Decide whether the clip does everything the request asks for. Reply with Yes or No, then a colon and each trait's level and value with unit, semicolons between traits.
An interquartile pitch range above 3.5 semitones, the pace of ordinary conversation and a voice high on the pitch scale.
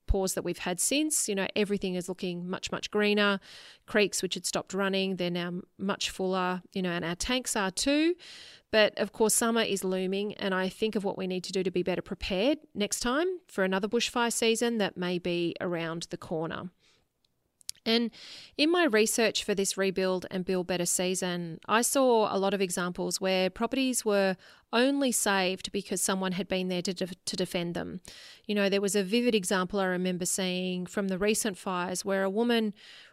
No: average, 2.9 semitones; average, 195 wpm; high, 195 Hz